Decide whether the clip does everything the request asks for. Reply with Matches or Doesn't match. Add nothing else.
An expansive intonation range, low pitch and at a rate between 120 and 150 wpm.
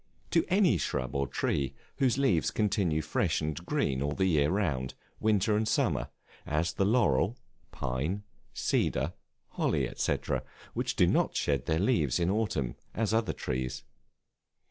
Matches